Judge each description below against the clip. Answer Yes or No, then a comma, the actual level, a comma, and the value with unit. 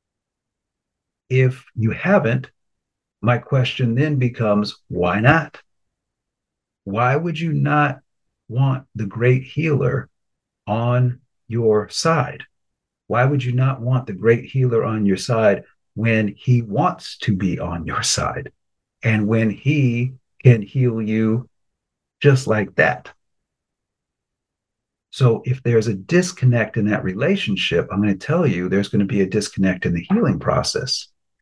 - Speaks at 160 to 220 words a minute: No, slow, 135 wpm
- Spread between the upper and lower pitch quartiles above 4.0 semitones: No, average, 3.7 semitones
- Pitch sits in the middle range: No, low, 120 Hz